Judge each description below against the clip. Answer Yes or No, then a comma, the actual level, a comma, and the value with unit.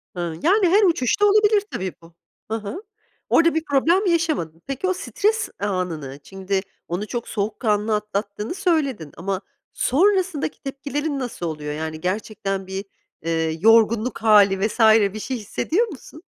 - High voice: Yes, high, 220 Hz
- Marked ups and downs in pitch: Yes, wide, 8.9 semitones